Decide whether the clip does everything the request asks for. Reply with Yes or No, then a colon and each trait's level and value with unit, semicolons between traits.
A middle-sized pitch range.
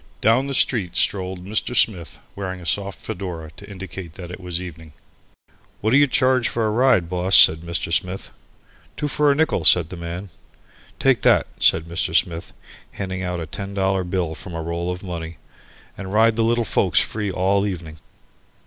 Yes: average, 3.7 semitones